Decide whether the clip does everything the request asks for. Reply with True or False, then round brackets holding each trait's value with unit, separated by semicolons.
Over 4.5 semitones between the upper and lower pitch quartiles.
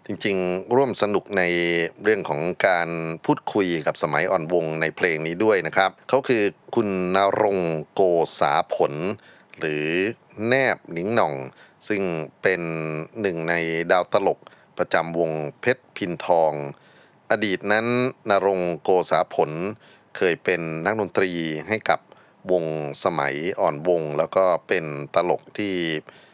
False (3.4 semitones)